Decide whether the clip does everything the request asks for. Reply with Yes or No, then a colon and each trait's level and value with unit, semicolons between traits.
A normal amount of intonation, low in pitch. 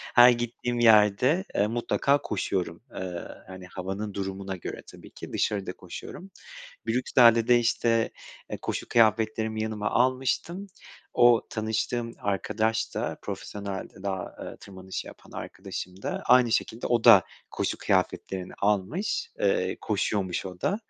Yes: average, 3.7 semitones; low, 110 Hz